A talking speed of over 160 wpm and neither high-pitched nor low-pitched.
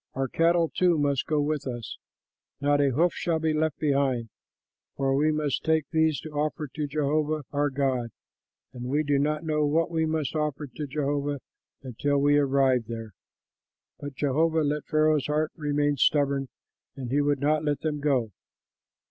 Yes: average, 170 wpm; medium, 145 Hz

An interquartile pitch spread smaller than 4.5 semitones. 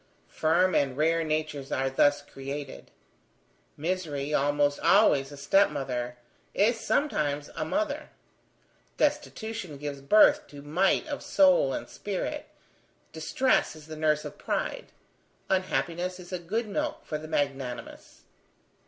No: average, 5.0 semitones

